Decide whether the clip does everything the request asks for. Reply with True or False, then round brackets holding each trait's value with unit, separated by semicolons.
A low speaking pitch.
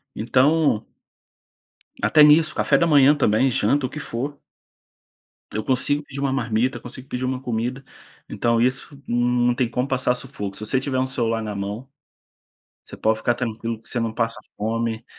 True (125 Hz)